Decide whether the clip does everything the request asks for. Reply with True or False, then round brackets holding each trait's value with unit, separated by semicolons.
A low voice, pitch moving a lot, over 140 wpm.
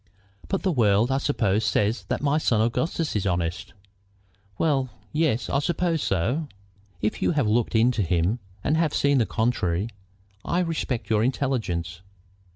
True (120 Hz; 5.9 semitones; 160 wpm)